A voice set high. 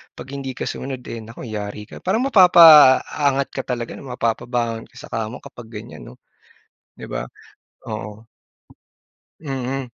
No: low, 125 Hz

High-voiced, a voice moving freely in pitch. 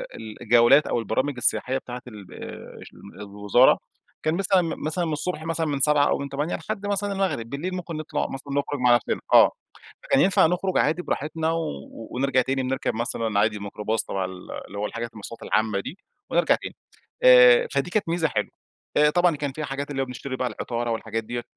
No: medium, 140 Hz; wide, 6.0 semitones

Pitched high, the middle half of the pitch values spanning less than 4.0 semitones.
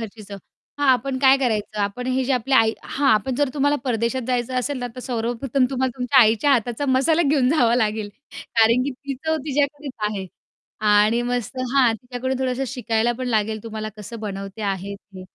Yes: high, 245 Hz; average, 3.3 semitones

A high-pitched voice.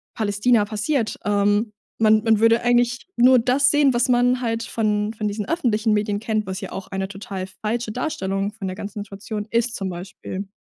Yes: high, 215 Hz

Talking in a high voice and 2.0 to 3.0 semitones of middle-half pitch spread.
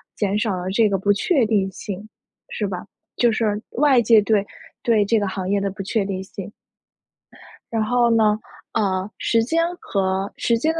Yes: high, 210 Hz; average, 2.7 semitones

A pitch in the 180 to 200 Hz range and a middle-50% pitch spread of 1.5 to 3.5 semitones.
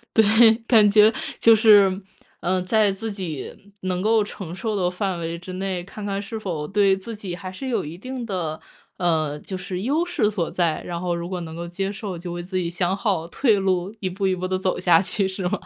Yes: high, 190 Hz; average, 2.9 semitones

